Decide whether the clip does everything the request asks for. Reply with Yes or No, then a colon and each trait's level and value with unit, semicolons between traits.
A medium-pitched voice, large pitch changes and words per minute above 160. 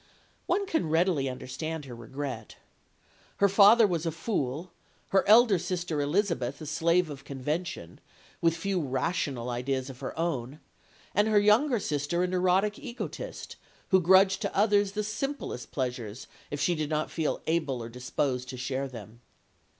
No: medium, 160 Hz; wide, 6.4 semitones; average, 155 wpm